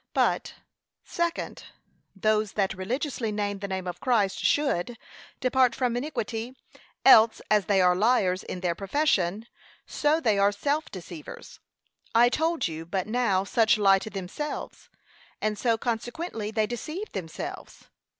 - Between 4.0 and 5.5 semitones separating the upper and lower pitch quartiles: Yes, average, 4.5 semitones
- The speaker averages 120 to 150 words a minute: Yes, average, 140 wpm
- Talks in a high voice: Yes, high, 215 Hz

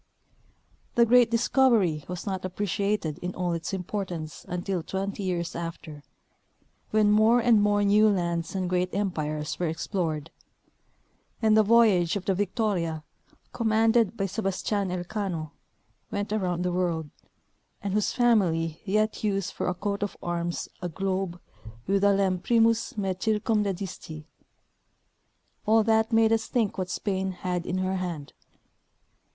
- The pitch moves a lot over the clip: No, average, 3.3 semitones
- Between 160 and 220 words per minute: No, average, 140 wpm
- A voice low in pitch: No, high, 195 Hz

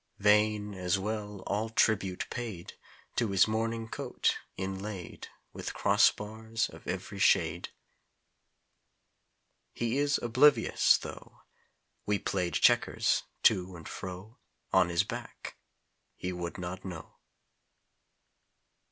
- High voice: No, low, 105 Hz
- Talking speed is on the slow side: Yes, slow, 105 wpm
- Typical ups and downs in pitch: Yes, average, 3.3 semitones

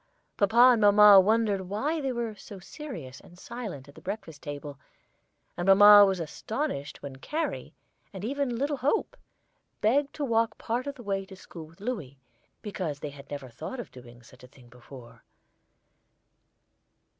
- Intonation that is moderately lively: No, wide, 8.6 semitones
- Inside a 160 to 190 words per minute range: Yes, average, 165 wpm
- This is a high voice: Yes, high, 200 Hz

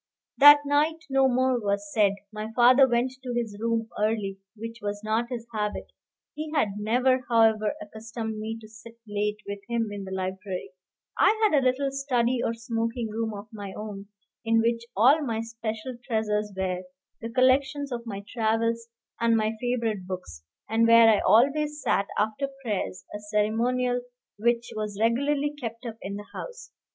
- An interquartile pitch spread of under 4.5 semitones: Yes, average, 3.0 semitones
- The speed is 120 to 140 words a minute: No, average, 170 wpm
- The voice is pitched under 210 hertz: No, high, 230 Hz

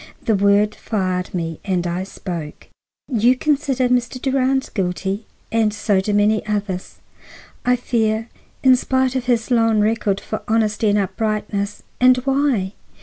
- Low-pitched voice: No, high, 215 Hz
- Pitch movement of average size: Yes, average, 3.8 semitones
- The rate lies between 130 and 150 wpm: Yes, average, 145 wpm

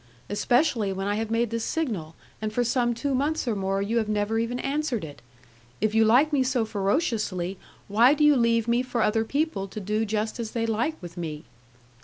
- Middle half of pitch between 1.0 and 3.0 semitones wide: No, average, 3.4 semitones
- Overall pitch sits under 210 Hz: No, high, 225 Hz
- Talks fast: Yes, fast, 210 wpm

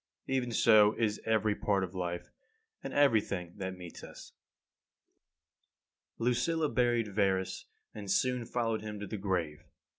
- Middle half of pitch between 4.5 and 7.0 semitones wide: No, average, 3.8 semitones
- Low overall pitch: Yes, low, 105 Hz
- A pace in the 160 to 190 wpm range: No, average, 140 wpm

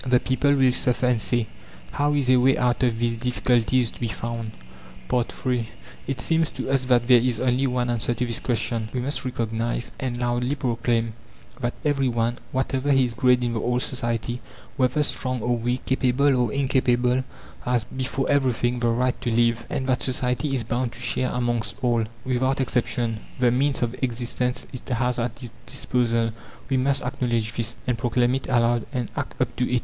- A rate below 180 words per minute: No, average, 190 wpm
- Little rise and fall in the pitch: Yes, narrow, 1.5 semitones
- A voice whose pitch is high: No, low, 125 Hz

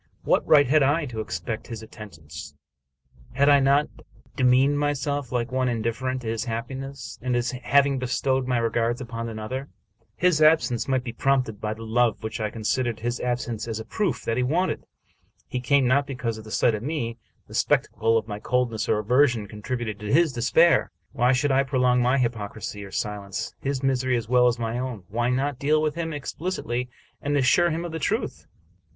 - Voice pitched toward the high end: No, low, 125 Hz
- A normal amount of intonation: Yes, average, 3.3 semitones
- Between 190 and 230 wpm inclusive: Yes, average, 195 wpm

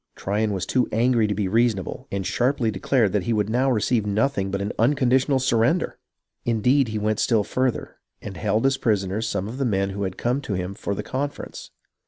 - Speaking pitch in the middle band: No, low, 110 Hz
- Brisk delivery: Yes, fast, 210 wpm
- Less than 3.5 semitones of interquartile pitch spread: No, average, 4.1 semitones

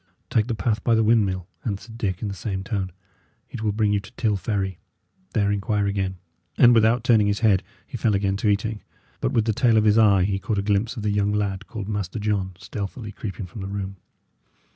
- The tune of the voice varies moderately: No, narrow, 2.1 semitones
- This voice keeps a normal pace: No, fast, 225 wpm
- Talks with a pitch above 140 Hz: No, low, 105 Hz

